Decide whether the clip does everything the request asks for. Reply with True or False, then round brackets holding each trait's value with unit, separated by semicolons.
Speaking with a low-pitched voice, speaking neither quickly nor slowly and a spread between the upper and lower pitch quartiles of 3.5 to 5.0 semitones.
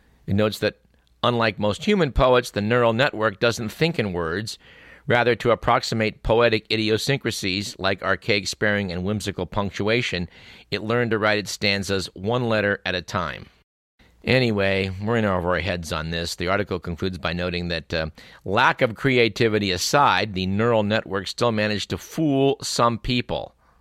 True (105 Hz; 160 wpm; 3.9 semitones)